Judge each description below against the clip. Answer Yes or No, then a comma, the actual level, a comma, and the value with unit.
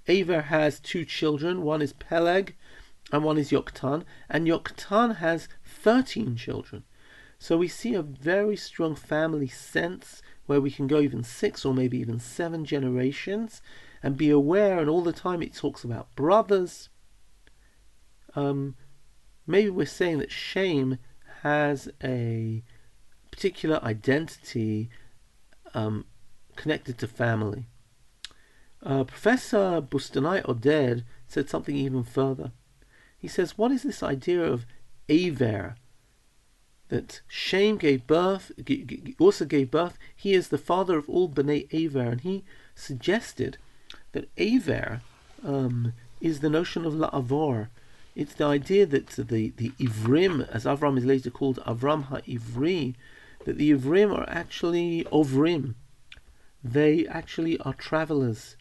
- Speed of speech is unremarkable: No, slow, 130 wpm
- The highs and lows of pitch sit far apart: No, average, 4.9 semitones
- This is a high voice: No, medium, 140 Hz